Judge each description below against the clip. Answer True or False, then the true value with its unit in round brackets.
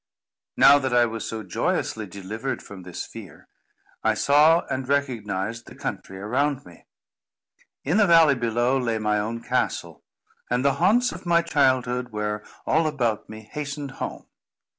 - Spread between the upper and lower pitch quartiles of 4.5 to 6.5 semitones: True (4.8 semitones)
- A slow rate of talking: False (155 wpm)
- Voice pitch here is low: True (125 Hz)